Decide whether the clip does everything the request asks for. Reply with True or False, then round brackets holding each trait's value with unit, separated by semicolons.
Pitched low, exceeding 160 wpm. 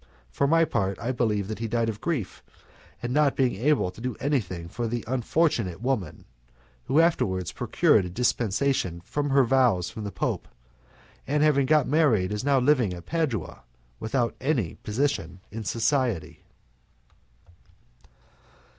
False (120 Hz; 145 wpm)